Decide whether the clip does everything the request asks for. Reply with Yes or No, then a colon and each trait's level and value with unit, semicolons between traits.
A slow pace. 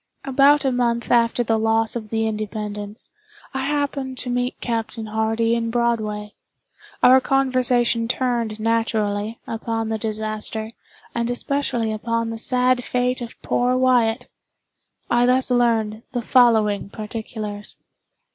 Yes: slow, 130 wpm